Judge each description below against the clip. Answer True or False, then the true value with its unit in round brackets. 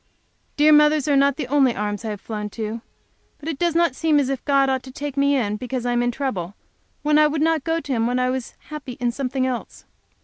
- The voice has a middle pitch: False (265 Hz)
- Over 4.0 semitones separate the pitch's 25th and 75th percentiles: False (3.5 semitones)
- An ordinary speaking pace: False (250 wpm)